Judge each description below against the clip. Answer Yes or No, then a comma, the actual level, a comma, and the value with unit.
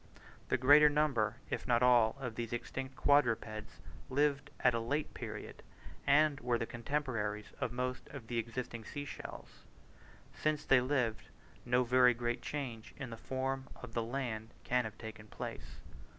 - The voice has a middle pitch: No, low, 125 Hz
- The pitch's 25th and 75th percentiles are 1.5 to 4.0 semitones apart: Yes, average, 3.0 semitones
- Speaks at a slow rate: No, average, 160 wpm